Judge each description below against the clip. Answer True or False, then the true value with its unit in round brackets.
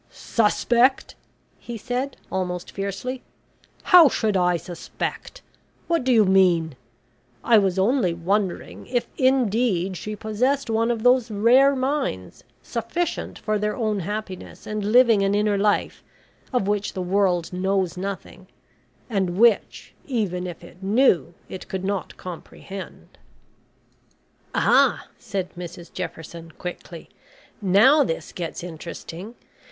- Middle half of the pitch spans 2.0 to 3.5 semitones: False (4.7 semitones)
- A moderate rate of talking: False (125 wpm)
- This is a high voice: True (200 Hz)